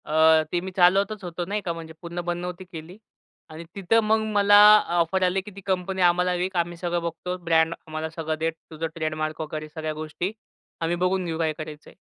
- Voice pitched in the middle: Yes, medium, 175 Hz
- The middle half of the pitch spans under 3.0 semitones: Yes, narrow, 2.5 semitones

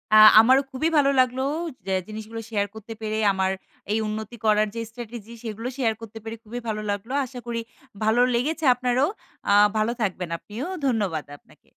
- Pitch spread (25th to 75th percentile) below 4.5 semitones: Yes, narrow, 2.5 semitones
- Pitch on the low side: No, high, 225 Hz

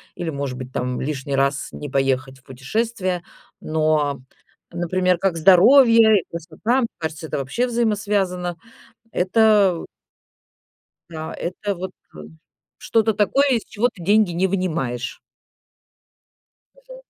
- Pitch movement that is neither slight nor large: No, wide, 6.3 semitones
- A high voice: No, medium, 180 Hz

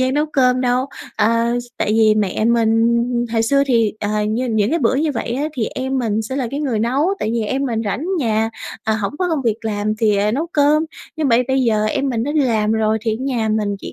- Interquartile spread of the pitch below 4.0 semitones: Yes, average, 3.4 semitones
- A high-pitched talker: Yes, high, 235 Hz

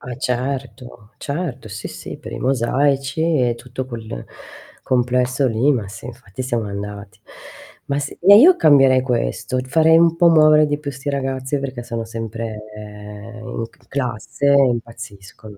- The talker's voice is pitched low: Yes, low, 125 Hz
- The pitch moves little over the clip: No, average, 3.7 semitones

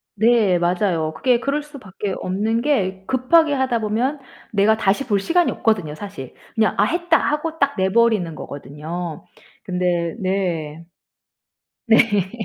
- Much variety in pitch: Yes, wide, 6.1 semitones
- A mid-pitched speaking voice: No, high, 205 Hz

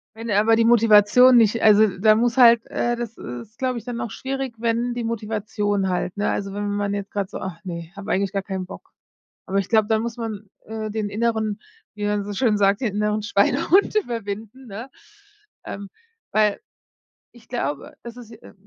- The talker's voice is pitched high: Yes, high, 215 Hz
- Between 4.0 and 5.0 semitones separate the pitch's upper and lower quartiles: No, narrow, 2.5 semitones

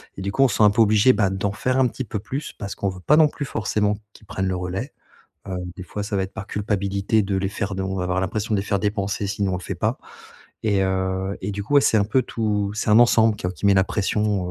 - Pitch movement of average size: No, narrow, 2.2 semitones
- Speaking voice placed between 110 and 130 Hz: No, low, 100 Hz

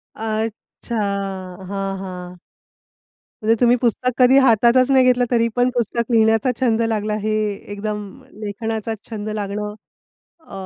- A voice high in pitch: Yes, high, 220 Hz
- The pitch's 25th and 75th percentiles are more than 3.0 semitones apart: No, average, 2.7 semitones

